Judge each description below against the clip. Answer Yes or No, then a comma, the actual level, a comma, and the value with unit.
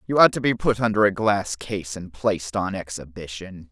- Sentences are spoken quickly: Yes, fast, 210 wpm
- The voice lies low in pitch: Yes, low, 100 Hz